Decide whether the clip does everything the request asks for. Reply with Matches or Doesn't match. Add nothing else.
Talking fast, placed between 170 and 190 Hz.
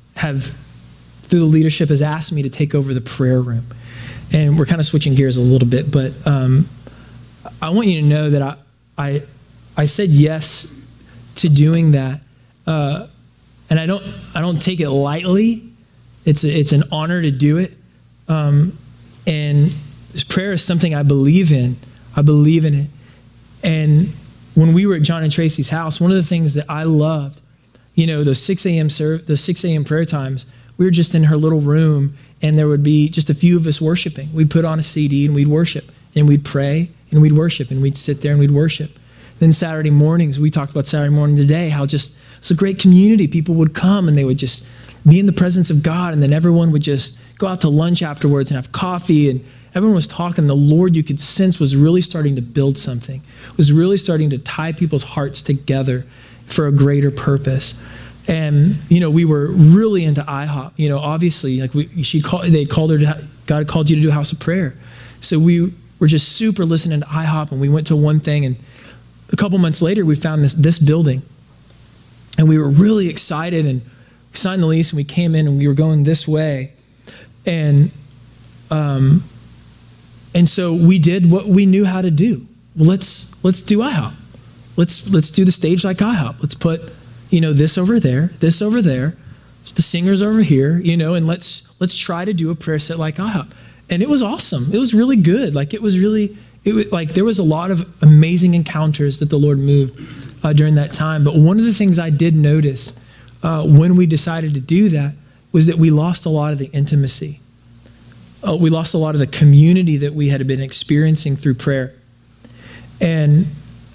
Doesn't match